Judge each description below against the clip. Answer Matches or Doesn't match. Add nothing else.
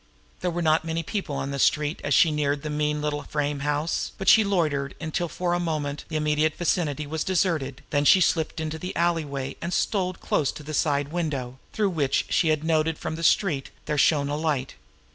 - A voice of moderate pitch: Matches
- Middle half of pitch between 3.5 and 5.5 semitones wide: Doesn't match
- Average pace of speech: Doesn't match